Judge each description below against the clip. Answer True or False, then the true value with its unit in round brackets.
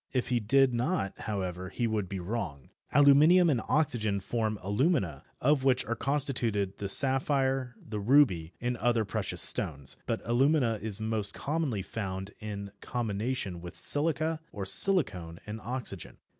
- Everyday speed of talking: True (145 wpm)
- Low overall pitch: True (115 Hz)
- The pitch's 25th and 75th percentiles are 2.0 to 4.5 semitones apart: False (5.3 semitones)